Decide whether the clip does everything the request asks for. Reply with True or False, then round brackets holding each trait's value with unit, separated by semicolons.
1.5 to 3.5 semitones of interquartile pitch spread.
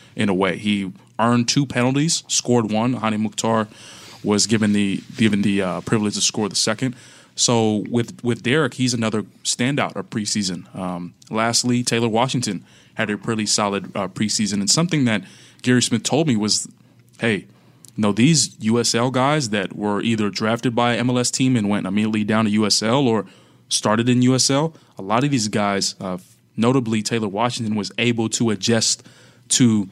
True (2.9 semitones)